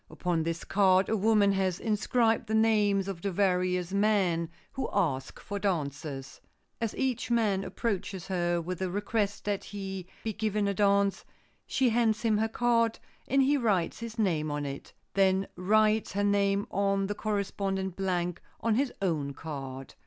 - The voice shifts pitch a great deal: No, average, 3.1 semitones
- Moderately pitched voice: No, high, 200 Hz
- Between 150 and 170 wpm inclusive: Yes, average, 165 wpm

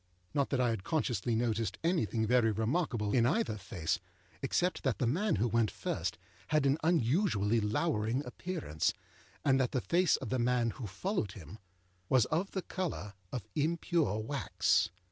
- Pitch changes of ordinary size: No, wide, 6.4 semitones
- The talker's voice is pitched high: No, low, 125 Hz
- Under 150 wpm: No, average, 165 wpm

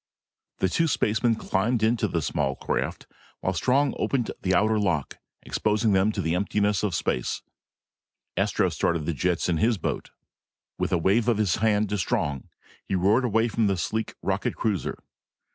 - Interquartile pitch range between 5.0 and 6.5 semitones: No, average, 3.8 semitones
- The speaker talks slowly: No, average, 175 wpm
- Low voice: Yes, low, 105 Hz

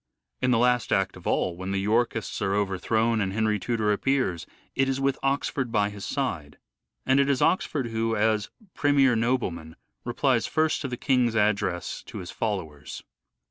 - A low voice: Yes, low, 110 Hz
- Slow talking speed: No, average, 175 wpm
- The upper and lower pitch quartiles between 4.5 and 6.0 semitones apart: Yes, average, 4.8 semitones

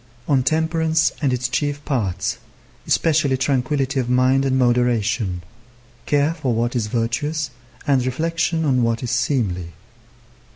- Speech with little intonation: No, average, 3.4 semitones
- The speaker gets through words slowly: Yes, slow, 130 wpm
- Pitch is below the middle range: Yes, low, 130 Hz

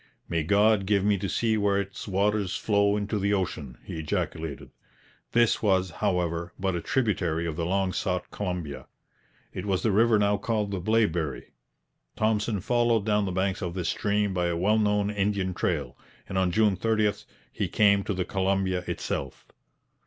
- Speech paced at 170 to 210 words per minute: Yes, average, 175 wpm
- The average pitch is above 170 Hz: No, low, 100 Hz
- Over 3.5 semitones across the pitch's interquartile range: No, narrow, 2.6 semitones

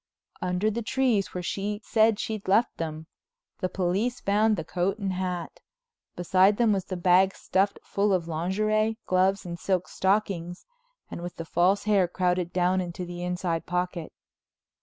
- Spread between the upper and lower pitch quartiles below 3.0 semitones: Yes, narrow, 2.5 semitones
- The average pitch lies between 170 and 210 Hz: Yes, medium, 185 Hz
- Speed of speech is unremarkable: Yes, average, 160 wpm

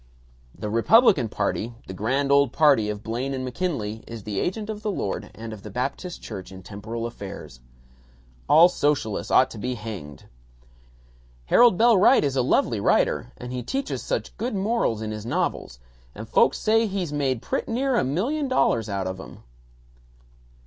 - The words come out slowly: No, average, 175 wpm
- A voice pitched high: No, low, 125 Hz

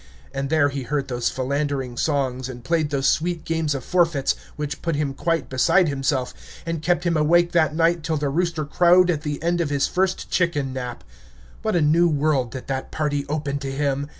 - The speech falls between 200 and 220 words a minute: Yes, fast, 205 wpm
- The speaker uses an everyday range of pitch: Yes, average, 3.4 semitones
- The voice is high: No, medium, 150 Hz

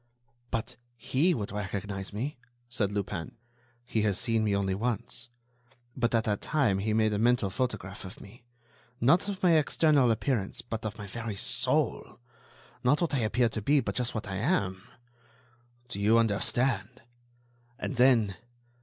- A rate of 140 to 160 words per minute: Yes, average, 155 wpm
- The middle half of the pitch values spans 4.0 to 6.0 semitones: No, average, 3.6 semitones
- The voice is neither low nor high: No, low, 115 Hz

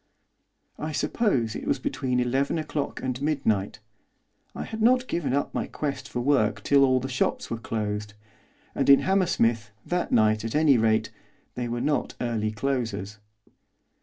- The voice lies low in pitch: Yes, low, 125 Hz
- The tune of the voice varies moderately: Yes, average, 4.7 semitones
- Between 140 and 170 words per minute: Yes, average, 160 wpm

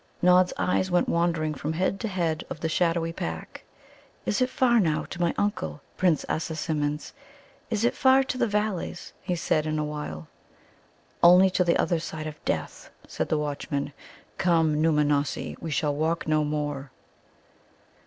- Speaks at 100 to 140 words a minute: No, average, 165 wpm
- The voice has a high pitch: No, medium, 160 Hz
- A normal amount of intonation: Yes, average, 3.2 semitones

